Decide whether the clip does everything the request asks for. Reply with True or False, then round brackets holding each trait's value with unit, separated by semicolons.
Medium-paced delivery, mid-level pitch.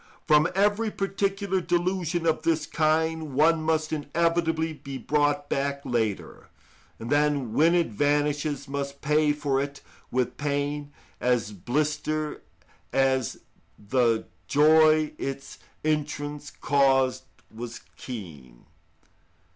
False (105 wpm; 145 Hz)